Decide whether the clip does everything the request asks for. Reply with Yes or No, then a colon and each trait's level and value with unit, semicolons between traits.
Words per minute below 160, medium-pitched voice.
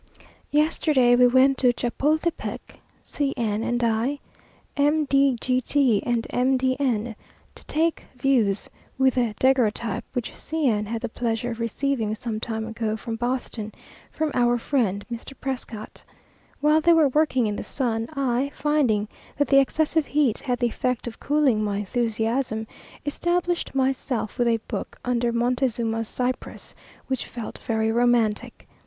No: average, 150 wpm; high, 245 Hz